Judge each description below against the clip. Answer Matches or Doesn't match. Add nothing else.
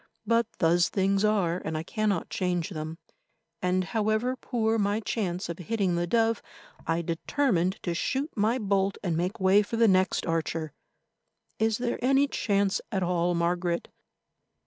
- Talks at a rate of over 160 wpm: Doesn't match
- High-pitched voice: Matches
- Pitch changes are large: Doesn't match